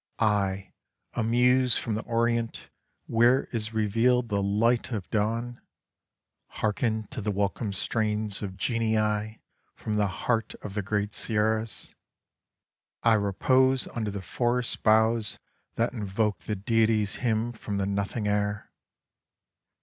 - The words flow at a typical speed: No, slow, 130 wpm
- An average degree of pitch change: No, narrow, 2.1 semitones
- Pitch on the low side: Yes, low, 110 Hz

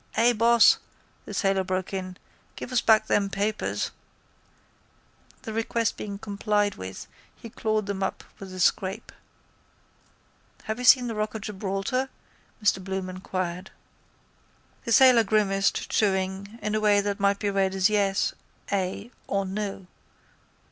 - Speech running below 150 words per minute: Yes, average, 140 wpm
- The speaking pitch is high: Yes, high, 200 Hz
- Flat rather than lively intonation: Yes, narrow, 2.1 semitones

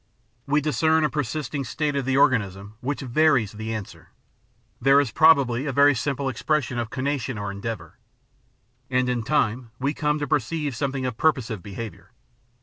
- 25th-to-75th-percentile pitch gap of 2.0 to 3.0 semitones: No, average, 4.4 semitones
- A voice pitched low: Yes, low, 130 Hz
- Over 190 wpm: No, average, 155 wpm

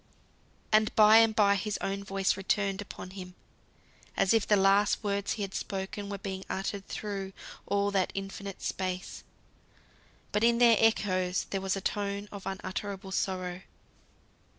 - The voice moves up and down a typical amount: No, narrow, 1.2 semitones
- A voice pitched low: No, high, 195 Hz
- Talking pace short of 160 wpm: Yes, average, 150 wpm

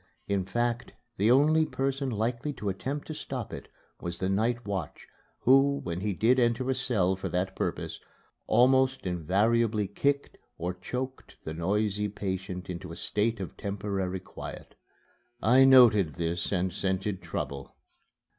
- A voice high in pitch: No, low, 105 Hz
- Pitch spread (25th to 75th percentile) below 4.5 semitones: No, average, 5.2 semitones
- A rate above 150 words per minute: No, average, 145 wpm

